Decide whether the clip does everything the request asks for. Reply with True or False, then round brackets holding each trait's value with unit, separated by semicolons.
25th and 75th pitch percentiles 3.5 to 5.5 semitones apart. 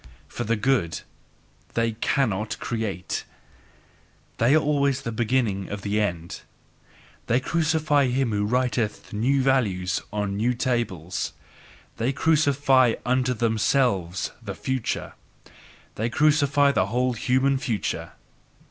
True (4.3 semitones)